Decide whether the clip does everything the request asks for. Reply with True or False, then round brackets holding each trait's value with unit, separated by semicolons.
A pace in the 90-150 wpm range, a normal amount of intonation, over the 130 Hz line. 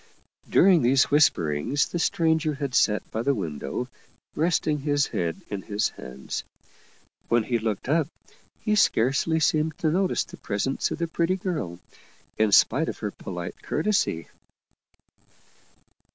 False (140 wpm; 7.5 semitones; 140 Hz)